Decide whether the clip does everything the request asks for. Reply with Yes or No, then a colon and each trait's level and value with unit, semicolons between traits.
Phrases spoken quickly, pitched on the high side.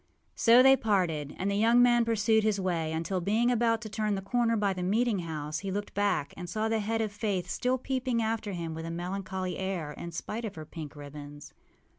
Yes: fast, 225 wpm; high, 200 Hz